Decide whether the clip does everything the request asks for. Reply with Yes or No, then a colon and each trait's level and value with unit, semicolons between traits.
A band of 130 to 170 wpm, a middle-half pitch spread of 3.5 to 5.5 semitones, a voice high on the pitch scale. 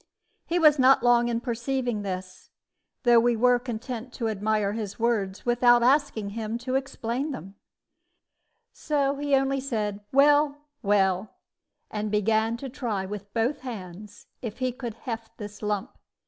Yes: average, 145 wpm; average, 3.8 semitones; high, 235 Hz